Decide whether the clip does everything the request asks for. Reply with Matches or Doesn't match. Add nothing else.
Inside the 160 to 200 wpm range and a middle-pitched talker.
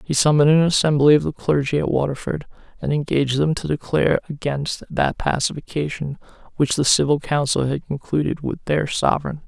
Matches